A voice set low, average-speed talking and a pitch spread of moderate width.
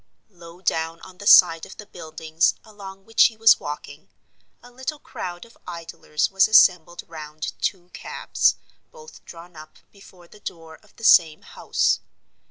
No: medium, 175 Hz; average, 160 wpm; average, 3.9 semitones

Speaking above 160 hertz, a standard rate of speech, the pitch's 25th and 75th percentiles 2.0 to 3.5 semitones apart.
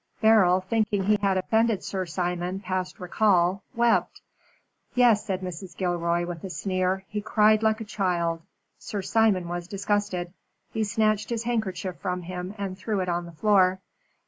Yes: high, 190 Hz; average, 160 wpm; average, 2.9 semitones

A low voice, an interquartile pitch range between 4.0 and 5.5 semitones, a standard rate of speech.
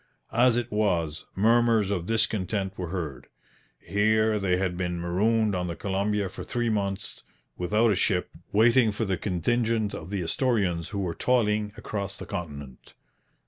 No: low, 100 Hz; average, 3.6 semitones; average, 155 wpm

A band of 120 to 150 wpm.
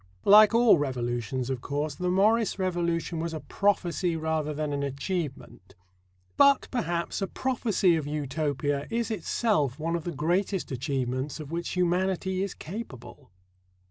Yes: average, 140 wpm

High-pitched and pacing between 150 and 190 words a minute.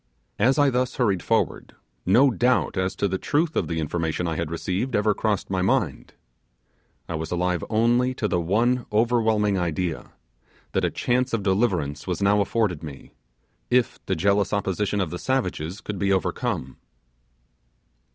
No: low, 100 Hz; average, 160 wpm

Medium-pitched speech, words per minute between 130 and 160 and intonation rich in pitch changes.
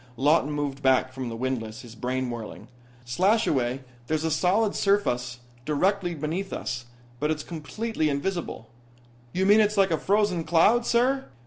Yes: medium, 155 Hz; average, 150 wpm; wide, 7.2 semitones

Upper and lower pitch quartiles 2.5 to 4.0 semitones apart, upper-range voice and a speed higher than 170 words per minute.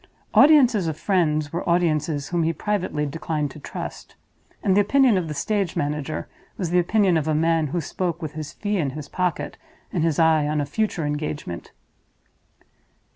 No: average, 3.5 semitones; medium, 165 Hz; average, 180 wpm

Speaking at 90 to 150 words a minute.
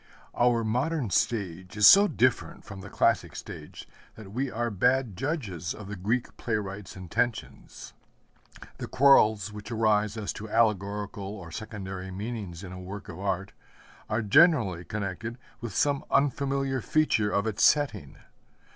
Yes: average, 145 wpm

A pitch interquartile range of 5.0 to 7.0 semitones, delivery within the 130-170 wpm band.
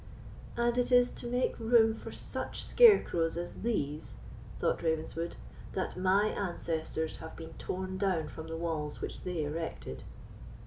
Yes: wide, 5.6 semitones; average, 145 wpm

